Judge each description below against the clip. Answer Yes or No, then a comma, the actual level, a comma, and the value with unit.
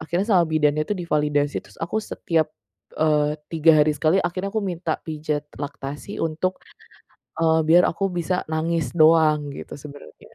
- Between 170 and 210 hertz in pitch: No, medium, 160 Hz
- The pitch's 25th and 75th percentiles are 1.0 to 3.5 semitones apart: Yes, narrow, 2.6 semitones